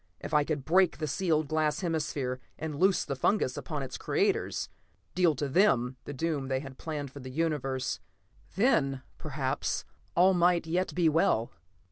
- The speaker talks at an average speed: Yes, average, 165 wpm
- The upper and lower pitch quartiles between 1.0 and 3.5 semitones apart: No, average, 4.0 semitones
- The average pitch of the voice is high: No, medium, 150 Hz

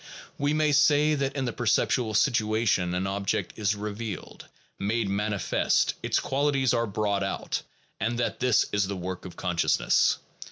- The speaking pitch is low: Yes, low, 110 Hz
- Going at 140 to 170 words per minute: Yes, average, 155 wpm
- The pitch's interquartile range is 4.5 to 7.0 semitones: Yes, average, 4.9 semitones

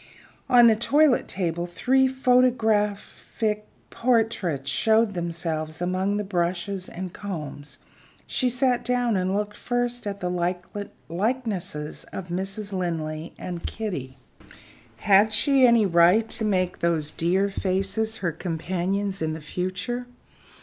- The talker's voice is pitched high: Yes, high, 195 Hz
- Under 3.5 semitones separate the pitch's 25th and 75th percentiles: No, average, 4.4 semitones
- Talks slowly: Yes, slow, 120 wpm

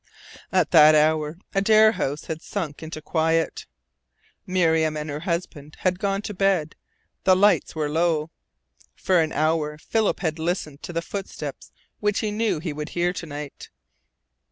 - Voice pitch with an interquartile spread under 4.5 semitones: Yes, average, 3.4 semitones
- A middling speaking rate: Yes, average, 155 wpm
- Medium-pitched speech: Yes, medium, 165 Hz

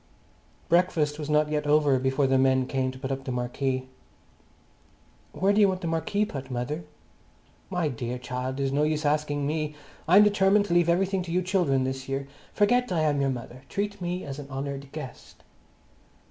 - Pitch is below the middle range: No, medium, 150 Hz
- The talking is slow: No, average, 190 wpm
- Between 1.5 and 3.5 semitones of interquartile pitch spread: No, average, 4.8 semitones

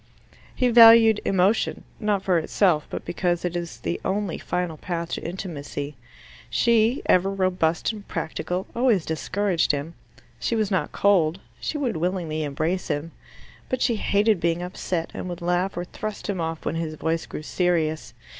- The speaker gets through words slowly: No, average, 165 wpm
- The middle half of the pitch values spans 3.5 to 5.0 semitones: Yes, average, 3.8 semitones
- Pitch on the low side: No, medium, 180 Hz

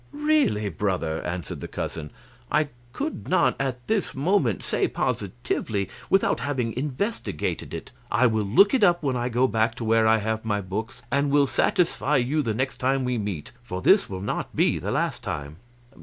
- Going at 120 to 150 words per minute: No, average, 185 wpm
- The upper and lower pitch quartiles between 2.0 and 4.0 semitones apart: No, wide, 5.4 semitones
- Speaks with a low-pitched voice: Yes, low, 120 Hz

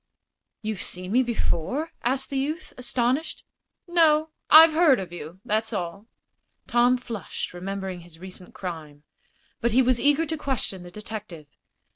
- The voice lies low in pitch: No, high, 225 Hz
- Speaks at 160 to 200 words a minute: No, average, 145 wpm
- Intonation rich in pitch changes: Yes, wide, 7.0 semitones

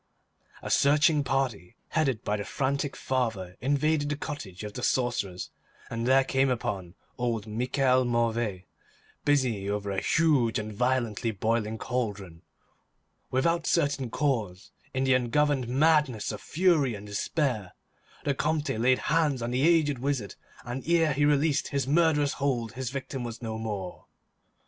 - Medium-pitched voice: No, low, 130 Hz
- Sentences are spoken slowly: No, average, 145 wpm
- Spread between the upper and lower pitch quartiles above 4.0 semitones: Yes, average, 4.6 semitones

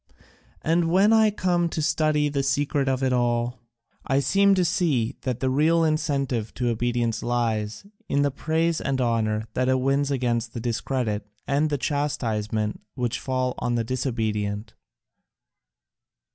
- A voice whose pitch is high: No, low, 130 Hz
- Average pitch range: Yes, average, 4.1 semitones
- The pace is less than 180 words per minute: Yes, average, 150 wpm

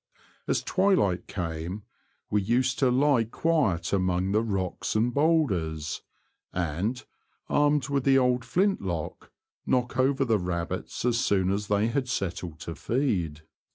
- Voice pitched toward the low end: Yes, low, 110 Hz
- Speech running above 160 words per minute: No, average, 140 wpm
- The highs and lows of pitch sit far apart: Yes, wide, 6.5 semitones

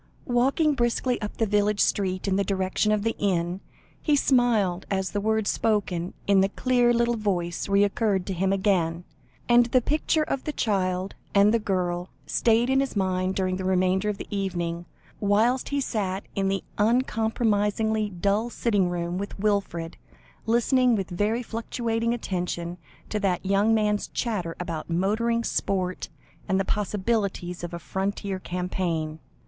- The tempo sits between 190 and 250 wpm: No, average, 155 wpm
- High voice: Yes, high, 200 Hz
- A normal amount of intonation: Yes, average, 3.5 semitones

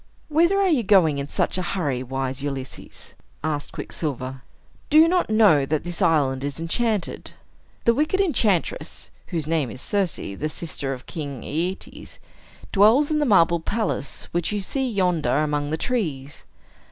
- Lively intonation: Yes, wide, 7.5 semitones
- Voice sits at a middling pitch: Yes, medium, 170 Hz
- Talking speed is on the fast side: No, average, 160 wpm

